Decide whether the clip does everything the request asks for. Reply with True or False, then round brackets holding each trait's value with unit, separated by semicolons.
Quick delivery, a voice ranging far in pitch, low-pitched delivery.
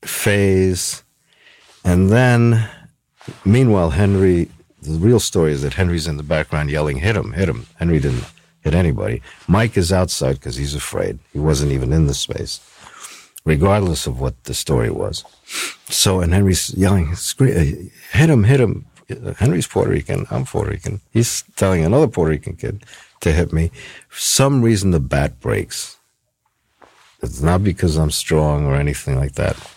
False (160 wpm; 6.1 semitones; 95 Hz)